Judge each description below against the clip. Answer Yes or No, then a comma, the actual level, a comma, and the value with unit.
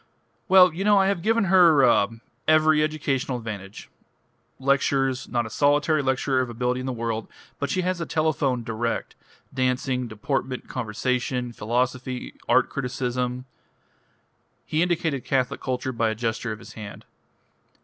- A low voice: Yes, low, 130 Hz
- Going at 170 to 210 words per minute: No, average, 150 wpm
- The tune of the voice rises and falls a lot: No, average, 4.0 semitones